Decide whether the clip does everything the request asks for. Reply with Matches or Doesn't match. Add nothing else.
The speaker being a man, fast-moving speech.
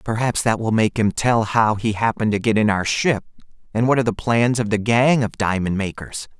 Matches